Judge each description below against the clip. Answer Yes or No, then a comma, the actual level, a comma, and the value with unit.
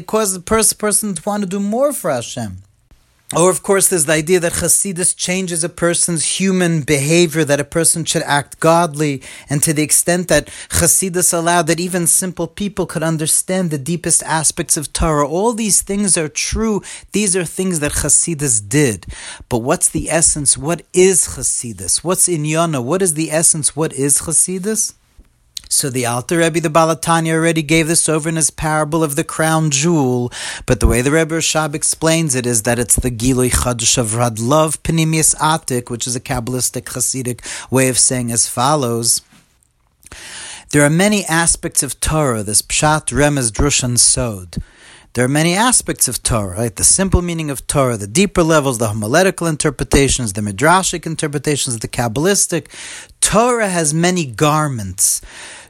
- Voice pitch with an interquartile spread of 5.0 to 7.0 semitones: Yes, average, 5.3 semitones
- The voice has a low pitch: No, medium, 155 Hz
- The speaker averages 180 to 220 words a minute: No, average, 170 wpm